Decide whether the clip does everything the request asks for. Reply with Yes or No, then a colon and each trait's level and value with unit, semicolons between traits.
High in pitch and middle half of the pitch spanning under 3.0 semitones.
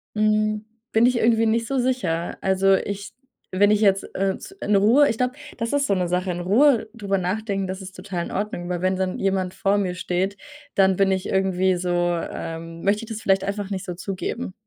Yes: high, 195 Hz; narrow, 2.5 semitones